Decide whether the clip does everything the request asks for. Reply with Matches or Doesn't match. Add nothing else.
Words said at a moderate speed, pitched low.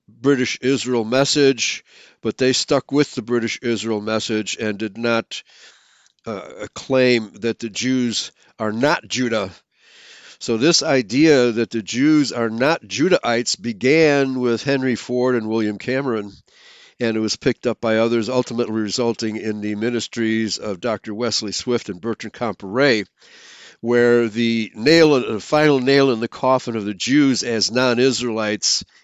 Matches